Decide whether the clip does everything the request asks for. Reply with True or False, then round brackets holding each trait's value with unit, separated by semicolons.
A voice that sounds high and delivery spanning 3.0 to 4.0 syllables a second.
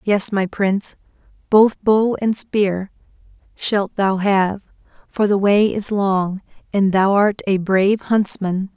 True (200 Hz; 3.6 syllables/s)